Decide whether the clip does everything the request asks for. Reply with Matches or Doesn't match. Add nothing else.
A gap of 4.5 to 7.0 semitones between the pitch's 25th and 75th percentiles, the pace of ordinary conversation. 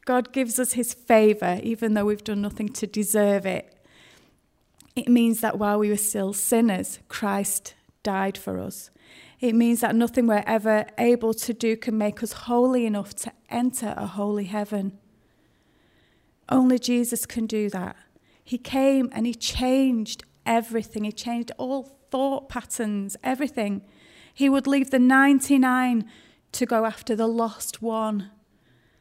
Doesn't match